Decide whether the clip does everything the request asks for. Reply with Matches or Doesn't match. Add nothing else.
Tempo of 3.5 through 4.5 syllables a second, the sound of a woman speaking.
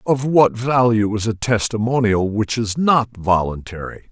Doesn't match